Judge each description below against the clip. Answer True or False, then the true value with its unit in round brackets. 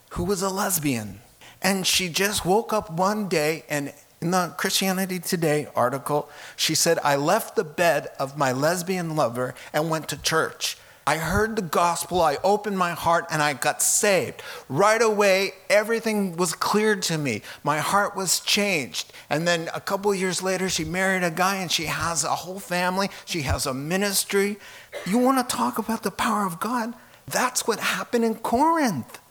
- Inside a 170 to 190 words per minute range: True (180 wpm)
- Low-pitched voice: False (185 Hz)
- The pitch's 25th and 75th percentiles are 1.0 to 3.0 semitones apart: False (4.4 semitones)